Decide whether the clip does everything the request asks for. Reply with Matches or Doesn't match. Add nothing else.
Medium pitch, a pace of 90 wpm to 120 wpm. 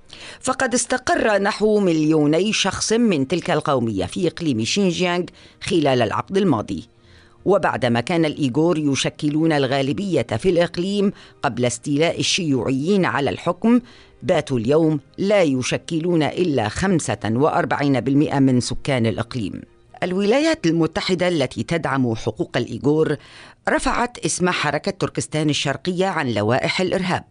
Matches